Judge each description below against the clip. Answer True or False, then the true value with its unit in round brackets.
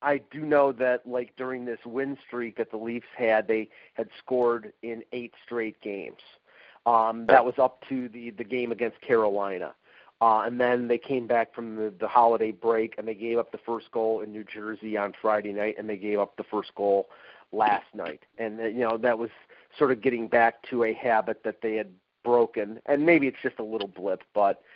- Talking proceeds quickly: True (210 wpm)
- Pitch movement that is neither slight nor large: False (2.1 semitones)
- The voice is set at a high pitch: False (115 Hz)